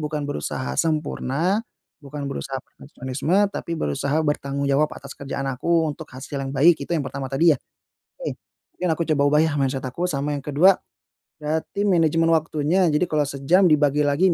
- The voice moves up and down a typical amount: Yes, average, 3.0 semitones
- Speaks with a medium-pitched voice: Yes, medium, 150 Hz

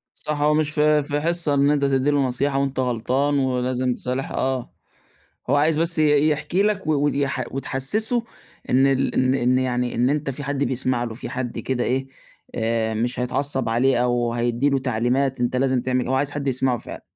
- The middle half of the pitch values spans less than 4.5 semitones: Yes, narrow, 2.6 semitones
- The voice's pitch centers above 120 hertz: Yes, low, 135 Hz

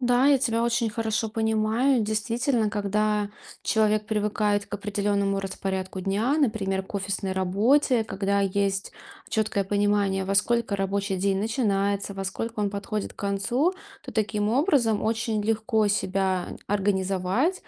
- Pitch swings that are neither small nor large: No, narrow, 2.2 semitones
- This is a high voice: Yes, high, 210 Hz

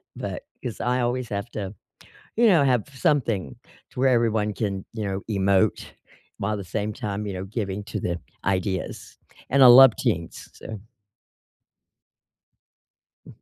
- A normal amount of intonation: Yes, average, 3.9 semitones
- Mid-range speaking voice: No, low, 105 Hz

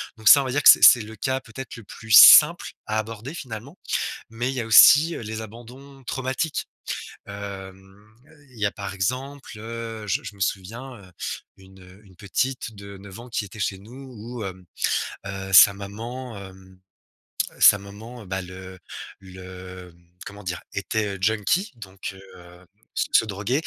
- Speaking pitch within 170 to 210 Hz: No, low, 105 Hz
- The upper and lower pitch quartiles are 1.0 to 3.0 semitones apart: No, average, 3.9 semitones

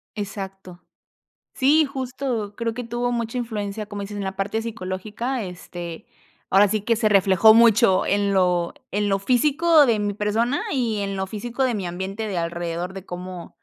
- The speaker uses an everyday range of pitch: Yes, average, 3.5 semitones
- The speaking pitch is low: No, high, 205 Hz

